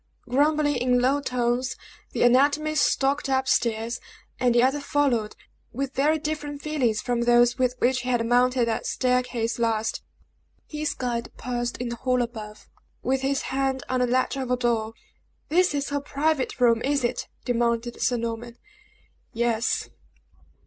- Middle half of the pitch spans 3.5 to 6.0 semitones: No, narrow, 2.6 semitones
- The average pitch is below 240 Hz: No, very high, 250 Hz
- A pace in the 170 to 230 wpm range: No, average, 155 wpm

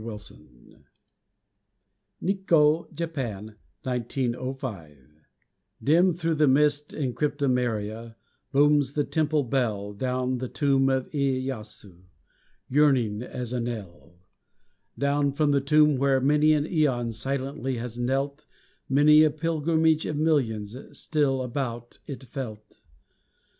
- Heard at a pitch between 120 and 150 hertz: Yes, low, 135 Hz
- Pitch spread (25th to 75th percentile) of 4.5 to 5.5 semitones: No, average, 3.8 semitones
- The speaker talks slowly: Yes, slow, 110 wpm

